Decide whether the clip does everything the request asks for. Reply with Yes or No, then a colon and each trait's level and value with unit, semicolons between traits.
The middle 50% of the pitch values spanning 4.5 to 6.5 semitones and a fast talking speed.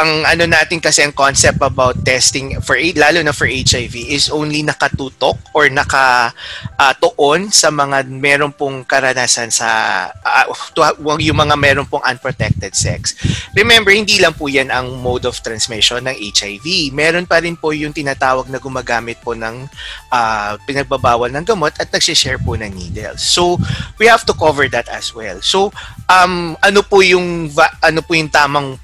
No: average, 4.1 semitones; fast, 165 wpm